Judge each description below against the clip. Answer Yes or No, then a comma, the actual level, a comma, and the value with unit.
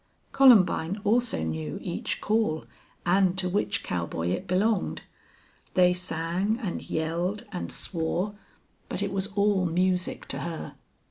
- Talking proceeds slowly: Yes, slow, 130 wpm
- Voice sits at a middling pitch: Yes, medium, 180 Hz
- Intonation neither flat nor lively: Yes, average, 3.7 semitones